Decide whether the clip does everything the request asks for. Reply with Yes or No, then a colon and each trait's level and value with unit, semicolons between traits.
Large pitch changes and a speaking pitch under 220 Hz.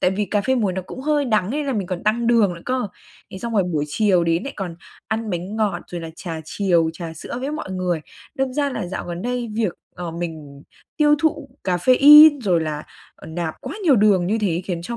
Yes: wide, 6.2 semitones; high, 195 Hz